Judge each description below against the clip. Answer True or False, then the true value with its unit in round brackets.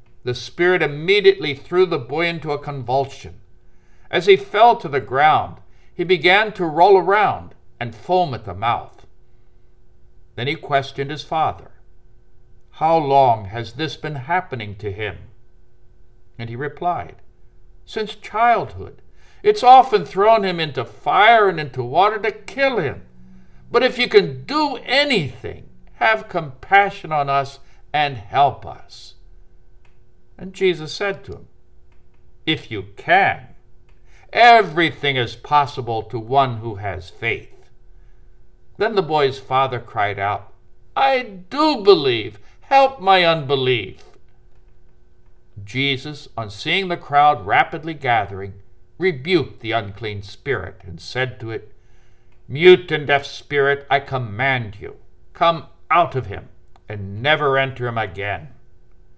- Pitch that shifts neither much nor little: False (7.9 semitones)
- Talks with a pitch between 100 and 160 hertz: True (140 Hz)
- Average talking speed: False (130 wpm)